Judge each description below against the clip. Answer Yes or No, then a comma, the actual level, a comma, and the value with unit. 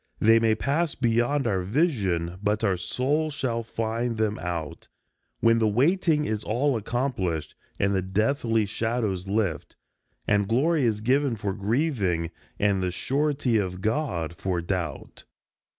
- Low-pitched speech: Yes, low, 110 Hz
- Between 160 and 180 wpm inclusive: No, average, 140 wpm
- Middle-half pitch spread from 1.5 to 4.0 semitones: No, average, 5.2 semitones